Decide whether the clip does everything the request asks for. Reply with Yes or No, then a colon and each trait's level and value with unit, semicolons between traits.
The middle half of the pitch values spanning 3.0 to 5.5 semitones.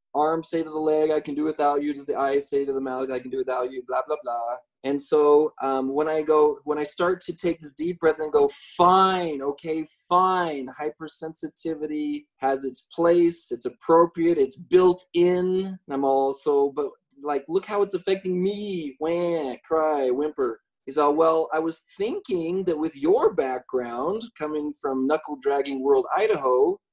Yes: average, 4.1 semitones